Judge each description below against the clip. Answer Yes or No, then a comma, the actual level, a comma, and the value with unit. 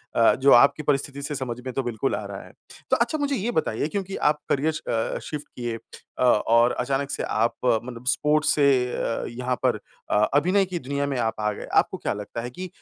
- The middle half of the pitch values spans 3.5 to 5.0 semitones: Yes, average, 4.1 semitones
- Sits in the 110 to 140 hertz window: Yes, low, 135 Hz